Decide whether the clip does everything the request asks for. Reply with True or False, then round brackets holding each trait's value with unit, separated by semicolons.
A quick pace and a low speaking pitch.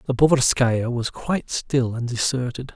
False (155 wpm; 125 Hz)